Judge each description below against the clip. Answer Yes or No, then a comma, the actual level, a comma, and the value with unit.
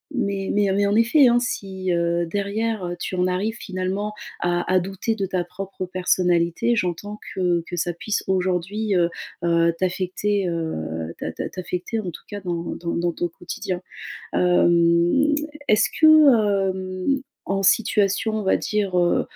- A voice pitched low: No, medium, 185 Hz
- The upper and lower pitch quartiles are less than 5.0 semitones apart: Yes, average, 2.7 semitones